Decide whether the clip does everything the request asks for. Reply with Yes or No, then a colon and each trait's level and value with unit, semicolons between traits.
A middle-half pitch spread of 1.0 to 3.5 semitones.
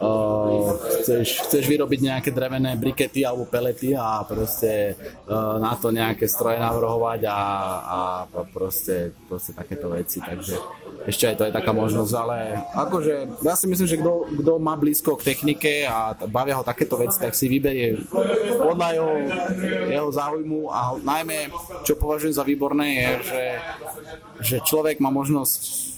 No: wide, 5.4 semitones